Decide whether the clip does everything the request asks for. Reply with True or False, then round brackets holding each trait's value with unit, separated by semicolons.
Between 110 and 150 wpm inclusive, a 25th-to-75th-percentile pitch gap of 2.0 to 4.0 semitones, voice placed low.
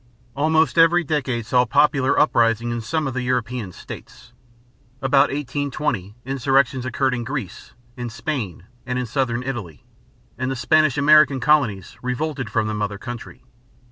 True (145 wpm; 3.5 semitones; 125 Hz)